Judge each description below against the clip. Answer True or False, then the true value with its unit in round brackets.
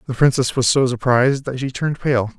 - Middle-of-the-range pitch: False (130 Hz)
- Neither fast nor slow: False (225 wpm)